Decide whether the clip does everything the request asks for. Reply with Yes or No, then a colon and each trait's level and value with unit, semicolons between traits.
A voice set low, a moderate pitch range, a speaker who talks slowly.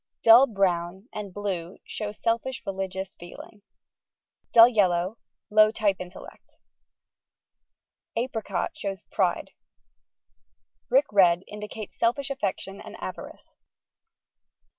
No: high, 205 Hz; average, 3.2 semitones; slow, 95 wpm